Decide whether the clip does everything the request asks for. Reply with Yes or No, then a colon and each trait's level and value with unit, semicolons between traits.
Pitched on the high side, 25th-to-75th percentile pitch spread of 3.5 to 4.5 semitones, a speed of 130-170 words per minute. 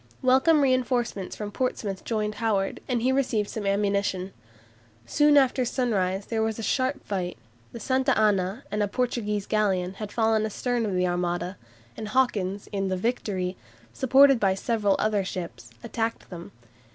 Yes: high, 215 Hz; average, 4.2 semitones; average, 155 wpm